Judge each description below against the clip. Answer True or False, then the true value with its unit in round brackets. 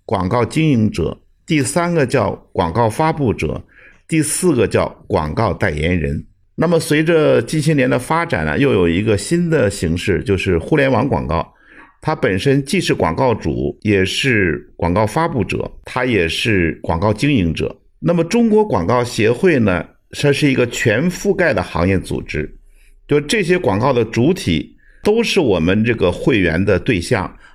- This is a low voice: True (125 Hz)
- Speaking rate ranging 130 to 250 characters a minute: True (245 characters per minute)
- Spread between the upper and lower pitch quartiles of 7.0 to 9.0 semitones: True (8.4 semitones)